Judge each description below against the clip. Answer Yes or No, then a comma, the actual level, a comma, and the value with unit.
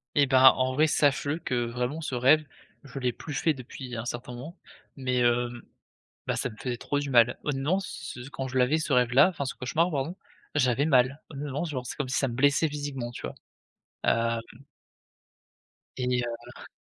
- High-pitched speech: No, low, 130 Hz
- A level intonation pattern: No, average, 3.0 semitones